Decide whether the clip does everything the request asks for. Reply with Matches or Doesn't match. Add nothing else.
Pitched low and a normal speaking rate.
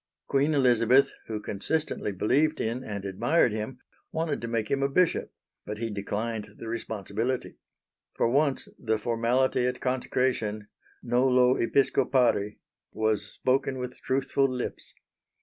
Doesn't match